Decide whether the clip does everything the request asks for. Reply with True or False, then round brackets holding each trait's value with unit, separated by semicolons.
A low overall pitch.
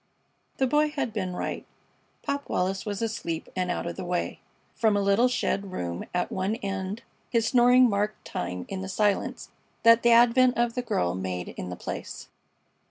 False (205 Hz)